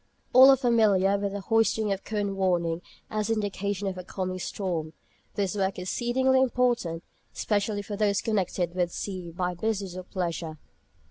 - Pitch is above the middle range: Yes, high, 200 Hz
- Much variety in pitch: No, average, 3.0 semitones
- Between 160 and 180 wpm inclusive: Yes, average, 165 wpm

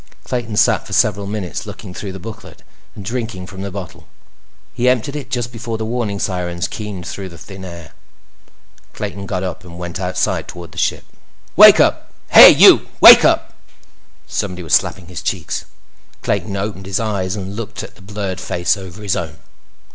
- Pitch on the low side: Yes, low, 100 Hz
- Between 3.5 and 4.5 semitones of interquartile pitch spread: No, average, 3.0 semitones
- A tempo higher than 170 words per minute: Yes, average, 180 wpm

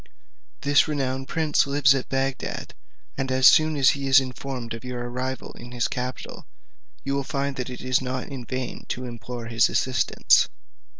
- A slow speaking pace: No, average, 175 wpm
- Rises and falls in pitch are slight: Yes, narrow, 1.7 semitones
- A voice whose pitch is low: Yes, low, 130 Hz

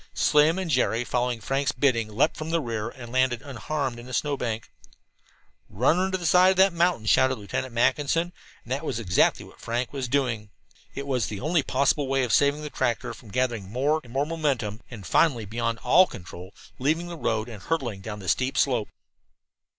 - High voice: No, low, 130 Hz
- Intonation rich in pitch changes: No, average, 4.5 semitones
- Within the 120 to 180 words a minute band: No, average, 200 wpm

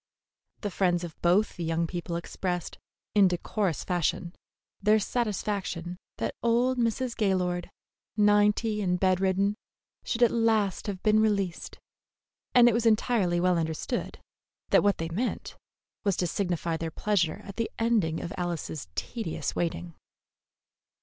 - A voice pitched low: No, high, 195 Hz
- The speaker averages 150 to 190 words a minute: No, average, 140 wpm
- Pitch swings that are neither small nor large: Yes, average, 3.7 semitones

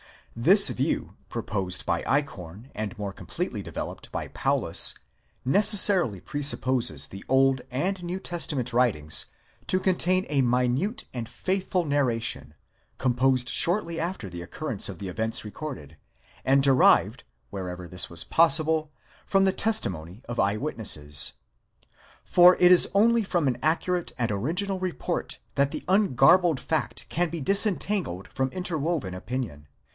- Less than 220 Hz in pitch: Yes, low, 135 Hz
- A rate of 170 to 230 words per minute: No, average, 140 wpm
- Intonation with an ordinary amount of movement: No, wide, 8.5 semitones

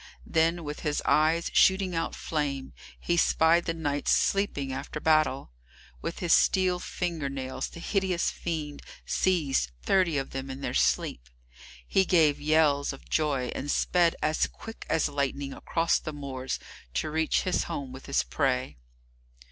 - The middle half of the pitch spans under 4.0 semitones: Yes, average, 3.6 semitones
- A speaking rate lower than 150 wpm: No, average, 155 wpm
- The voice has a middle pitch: Yes, medium, 155 Hz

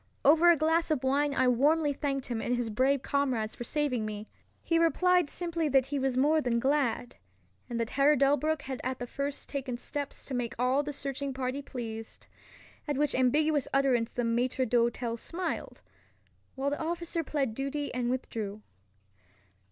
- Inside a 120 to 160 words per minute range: No, average, 175 wpm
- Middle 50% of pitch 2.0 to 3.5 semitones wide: Yes, average, 3.2 semitones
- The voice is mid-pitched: No, very high, 270 Hz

